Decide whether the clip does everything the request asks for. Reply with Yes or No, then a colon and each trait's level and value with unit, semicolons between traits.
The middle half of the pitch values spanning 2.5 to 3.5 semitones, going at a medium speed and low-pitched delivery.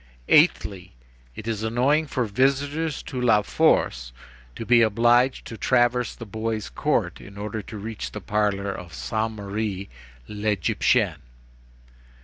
No: average, 3.2 semitones; slow, 130 wpm; low, 110 Hz